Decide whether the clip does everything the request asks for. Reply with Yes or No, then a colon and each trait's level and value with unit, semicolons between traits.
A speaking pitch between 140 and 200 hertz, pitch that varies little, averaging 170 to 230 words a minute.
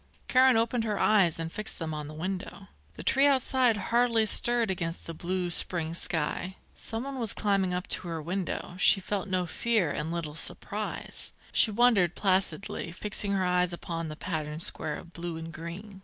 No: medium, 185 Hz; average, 4.4 semitones; average, 180 wpm